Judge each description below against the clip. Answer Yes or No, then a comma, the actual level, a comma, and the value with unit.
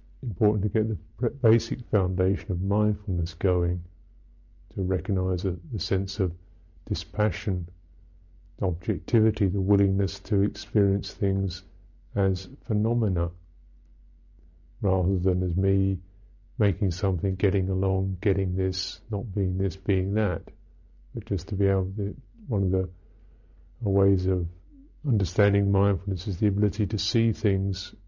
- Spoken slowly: Yes, slow, 125 wpm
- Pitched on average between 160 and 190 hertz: No, very low, 95 Hz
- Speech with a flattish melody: Yes, narrow, 2.2 semitones